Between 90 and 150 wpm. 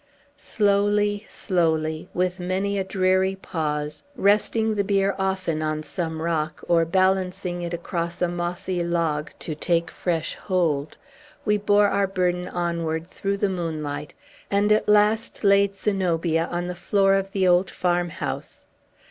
Yes: average, 140 wpm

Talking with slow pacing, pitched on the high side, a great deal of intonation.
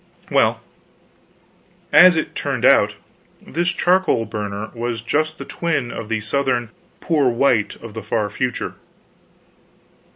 No: slow, 125 wpm; low, 120 Hz; wide, 5.9 semitones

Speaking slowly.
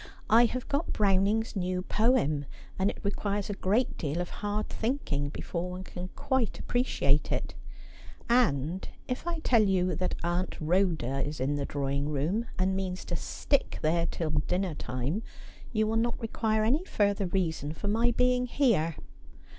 No: average, 165 wpm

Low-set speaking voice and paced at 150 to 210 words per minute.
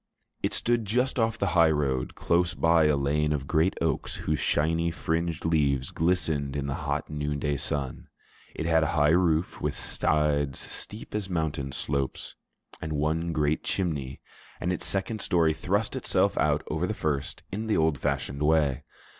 Yes: very low, 80 Hz; average, 170 wpm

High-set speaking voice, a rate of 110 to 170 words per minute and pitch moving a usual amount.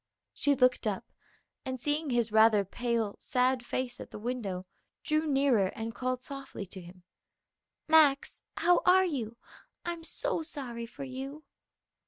Yes: very high, 255 Hz; average, 145 wpm; average, 4.2 semitones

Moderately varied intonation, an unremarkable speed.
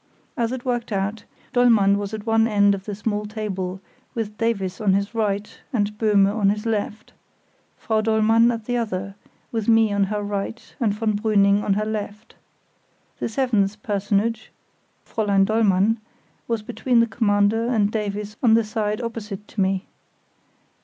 No: narrow, 1.9 semitones; average, 160 wpm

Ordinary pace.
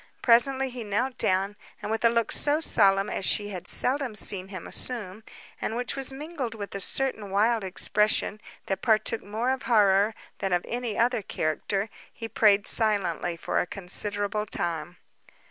Yes: average, 165 wpm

